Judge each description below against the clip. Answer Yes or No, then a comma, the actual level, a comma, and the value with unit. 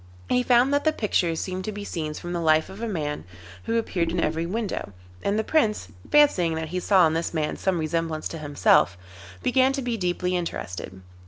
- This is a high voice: No, medium, 180 Hz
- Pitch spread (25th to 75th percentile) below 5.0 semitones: No, wide, 5.5 semitones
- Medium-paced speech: No, fast, 210 wpm